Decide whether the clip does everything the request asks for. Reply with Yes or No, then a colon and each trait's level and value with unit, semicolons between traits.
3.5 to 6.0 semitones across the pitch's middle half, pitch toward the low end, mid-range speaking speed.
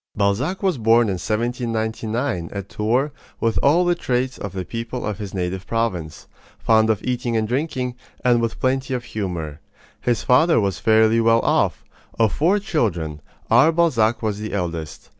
Yes: average, 3.9 semitones; low, 115 Hz; average, 165 wpm